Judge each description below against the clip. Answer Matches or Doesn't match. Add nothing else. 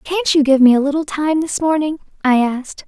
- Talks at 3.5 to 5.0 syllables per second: Doesn't match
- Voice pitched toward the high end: Matches